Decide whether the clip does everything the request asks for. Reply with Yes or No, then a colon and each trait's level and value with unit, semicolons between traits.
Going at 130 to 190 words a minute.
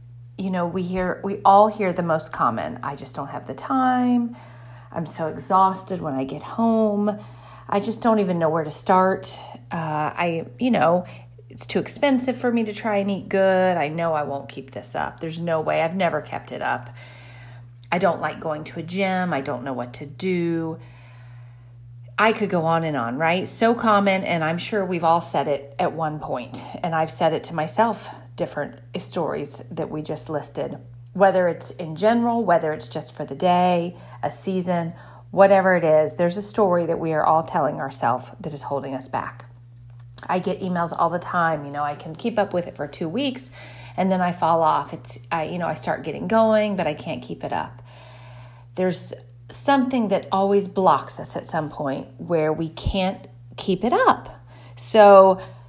No: average, 200 wpm